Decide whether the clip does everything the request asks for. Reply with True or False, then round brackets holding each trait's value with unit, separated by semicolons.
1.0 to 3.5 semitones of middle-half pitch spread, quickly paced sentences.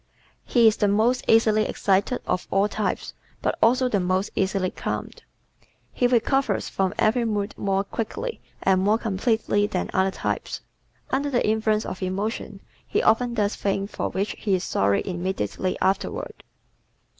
False (2.9 semitones; 155 wpm)